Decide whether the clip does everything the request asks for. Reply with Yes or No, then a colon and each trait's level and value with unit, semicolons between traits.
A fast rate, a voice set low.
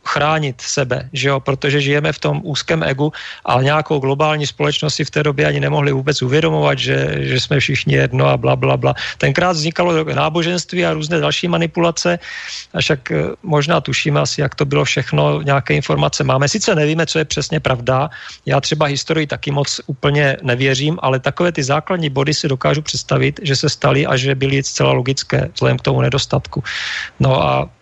No: fast, 185 wpm; medium, 145 Hz